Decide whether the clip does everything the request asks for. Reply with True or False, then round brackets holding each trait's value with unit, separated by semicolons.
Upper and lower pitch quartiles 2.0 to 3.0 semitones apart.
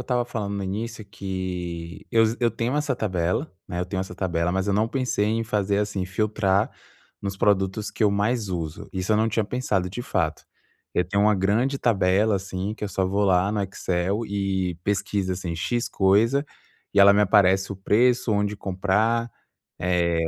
True (2.6 semitones)